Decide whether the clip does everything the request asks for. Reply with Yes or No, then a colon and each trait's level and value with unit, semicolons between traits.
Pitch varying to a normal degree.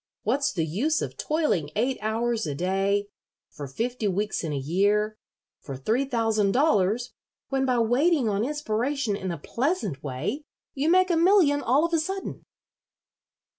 No: wide, 6.5 semitones